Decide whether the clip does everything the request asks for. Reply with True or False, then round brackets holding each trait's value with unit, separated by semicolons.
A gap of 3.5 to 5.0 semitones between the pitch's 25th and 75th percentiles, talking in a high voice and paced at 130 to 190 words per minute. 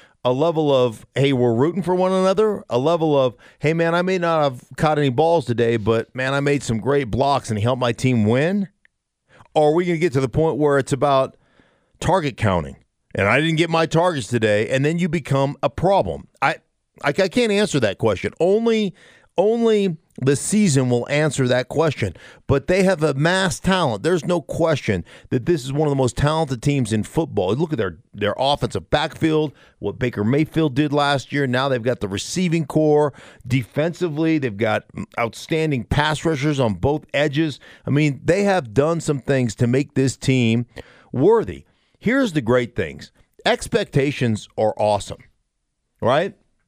False (4.6 semitones; 145 Hz; 185 wpm)